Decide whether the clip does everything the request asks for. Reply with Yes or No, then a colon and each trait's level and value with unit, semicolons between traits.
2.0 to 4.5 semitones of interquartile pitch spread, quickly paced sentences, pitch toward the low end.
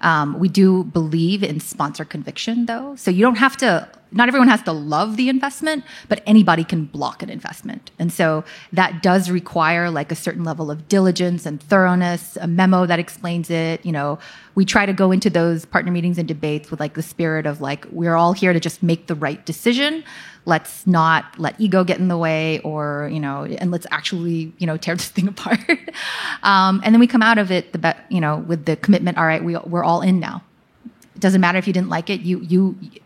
No: average, 3.3 semitones; fast, 225 wpm; medium, 175 Hz